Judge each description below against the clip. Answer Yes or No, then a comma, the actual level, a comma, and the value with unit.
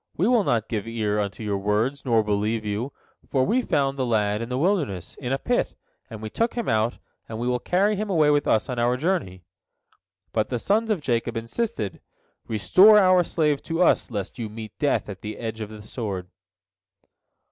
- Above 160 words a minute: Yes, average, 200 wpm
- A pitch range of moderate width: No, wide, 7.0 semitones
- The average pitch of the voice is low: Yes, low, 120 Hz